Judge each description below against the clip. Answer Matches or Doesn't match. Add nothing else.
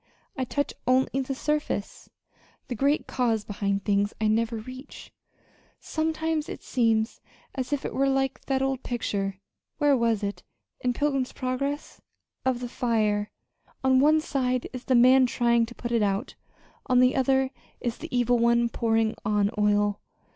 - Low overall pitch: Doesn't match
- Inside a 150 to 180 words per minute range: Matches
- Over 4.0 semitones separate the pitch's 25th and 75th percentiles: Doesn't match